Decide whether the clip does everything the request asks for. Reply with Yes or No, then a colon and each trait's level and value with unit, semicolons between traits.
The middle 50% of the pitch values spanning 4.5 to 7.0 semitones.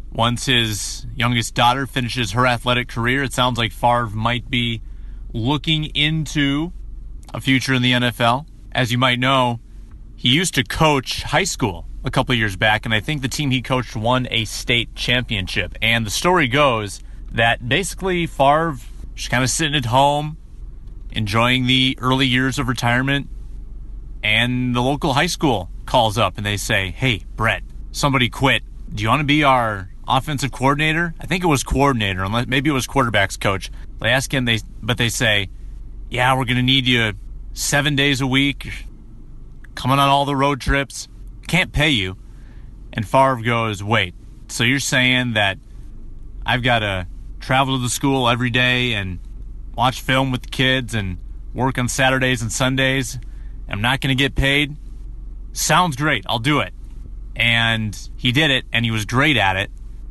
No: average, 3.3 semitones